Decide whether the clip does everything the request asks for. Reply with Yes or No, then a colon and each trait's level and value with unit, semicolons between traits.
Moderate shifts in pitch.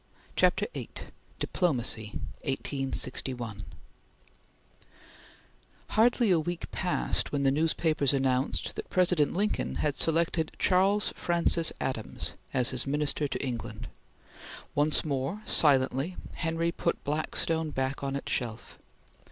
Yes: average, 4.1 semitones